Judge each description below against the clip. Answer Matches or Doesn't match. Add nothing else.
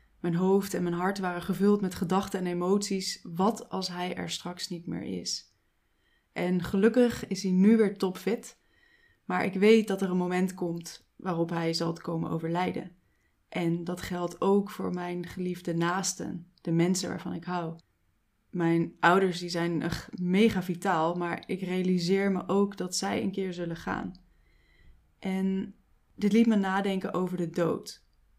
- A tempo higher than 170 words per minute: Doesn't match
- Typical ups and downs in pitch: Doesn't match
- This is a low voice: Doesn't match